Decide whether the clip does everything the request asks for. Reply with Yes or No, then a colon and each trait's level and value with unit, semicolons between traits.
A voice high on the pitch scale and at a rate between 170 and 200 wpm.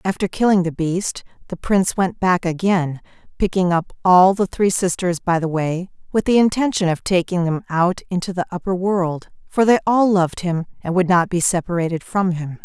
No: medium, 180 Hz; average, 195 wpm